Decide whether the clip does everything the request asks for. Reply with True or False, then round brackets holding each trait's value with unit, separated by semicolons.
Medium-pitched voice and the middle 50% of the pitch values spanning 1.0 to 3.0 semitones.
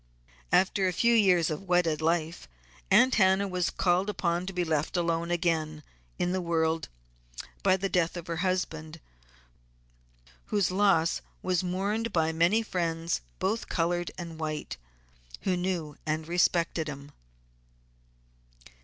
True (175 Hz; 2.5 semitones)